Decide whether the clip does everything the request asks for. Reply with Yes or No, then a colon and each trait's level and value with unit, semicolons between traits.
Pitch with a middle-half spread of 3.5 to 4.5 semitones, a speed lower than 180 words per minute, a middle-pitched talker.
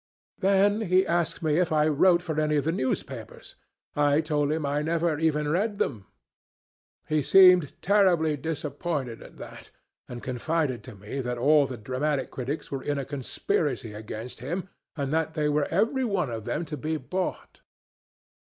Yes: average, 4.1 semitones; average, 170 wpm; medium, 150 Hz